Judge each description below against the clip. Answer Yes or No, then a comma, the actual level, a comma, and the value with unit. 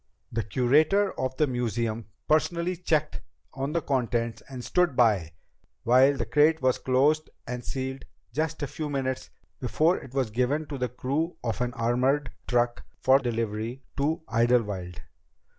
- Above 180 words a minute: No, average, 150 wpm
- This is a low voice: Yes, low, 130 Hz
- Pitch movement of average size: Yes, average, 3.9 semitones